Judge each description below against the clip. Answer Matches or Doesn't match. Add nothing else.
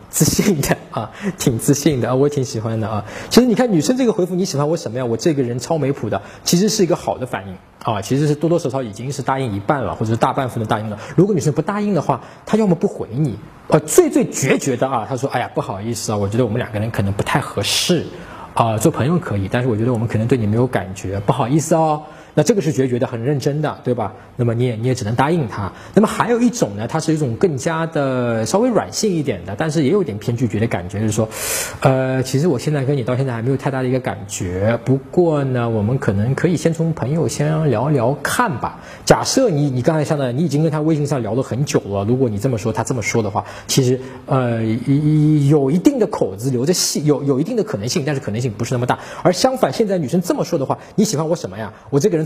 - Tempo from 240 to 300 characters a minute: Doesn't match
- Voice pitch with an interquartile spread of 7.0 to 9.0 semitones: Doesn't match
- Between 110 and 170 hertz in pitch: Matches